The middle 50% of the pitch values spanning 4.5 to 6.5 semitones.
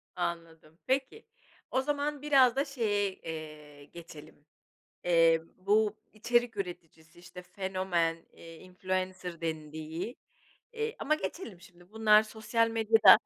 Yes: wide, 5.5 semitones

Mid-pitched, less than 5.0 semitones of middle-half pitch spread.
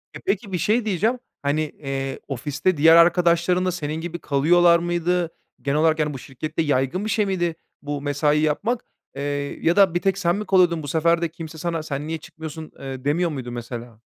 Yes: medium, 160 Hz; average, 3.3 semitones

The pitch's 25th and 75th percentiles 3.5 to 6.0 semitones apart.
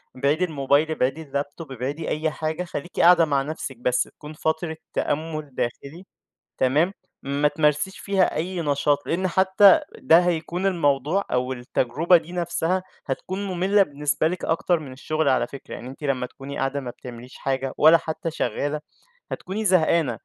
Yes: average, 3.9 semitones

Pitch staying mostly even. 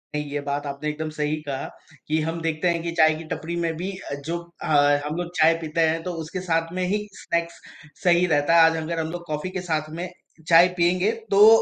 Yes: narrow, 2.1 semitones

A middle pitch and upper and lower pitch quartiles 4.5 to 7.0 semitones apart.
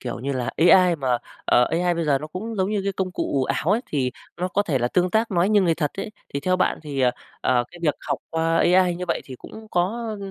Yes: medium, 175 Hz; average, 5.2 semitones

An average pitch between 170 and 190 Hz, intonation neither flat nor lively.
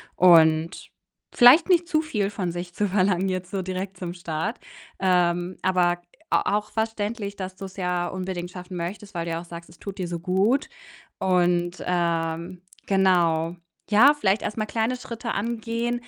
Yes: medium, 185 Hz; average, 3.1 semitones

